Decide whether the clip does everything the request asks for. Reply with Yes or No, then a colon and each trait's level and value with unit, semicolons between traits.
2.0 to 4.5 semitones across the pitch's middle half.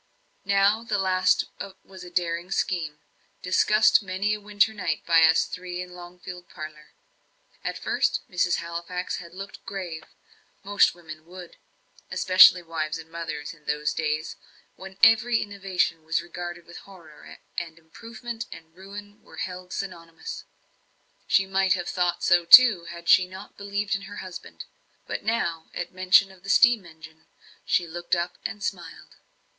Yes: average, 2.8 semitones